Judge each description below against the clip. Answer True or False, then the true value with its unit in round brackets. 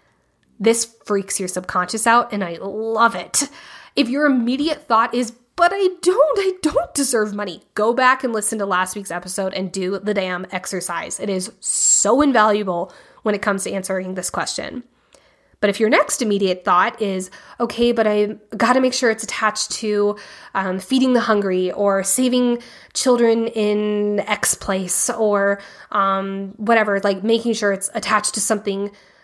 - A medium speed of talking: True (165 wpm)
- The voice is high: True (210 Hz)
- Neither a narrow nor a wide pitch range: True (3.3 semitones)